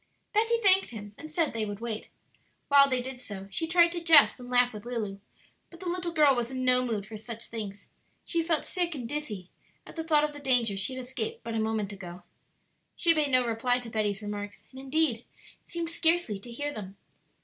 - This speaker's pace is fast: Yes, fast, 215 wpm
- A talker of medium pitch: No, very high, 250 Hz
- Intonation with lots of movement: Yes, wide, 6.2 semitones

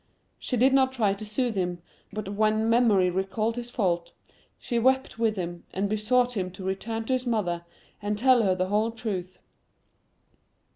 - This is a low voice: No, high, 215 Hz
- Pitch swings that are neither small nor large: Yes, average, 3.9 semitones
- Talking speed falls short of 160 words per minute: No, average, 175 wpm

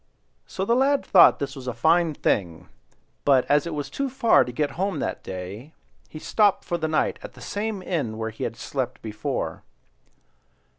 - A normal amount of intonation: No, wide, 8.2 semitones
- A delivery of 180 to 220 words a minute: Yes, average, 190 wpm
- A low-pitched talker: No, medium, 150 Hz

